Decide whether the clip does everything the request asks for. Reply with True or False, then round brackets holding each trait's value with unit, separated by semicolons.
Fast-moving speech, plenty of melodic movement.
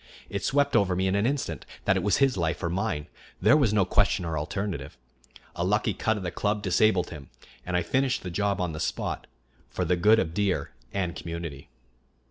False (220 wpm; 3.3 semitones)